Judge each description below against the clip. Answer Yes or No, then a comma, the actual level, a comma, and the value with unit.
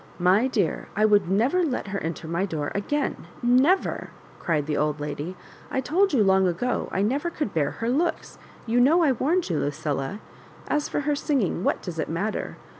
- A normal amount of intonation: No, wide, 9.0 semitones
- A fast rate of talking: Yes, fast, 215 wpm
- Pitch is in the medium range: No, high, 210 Hz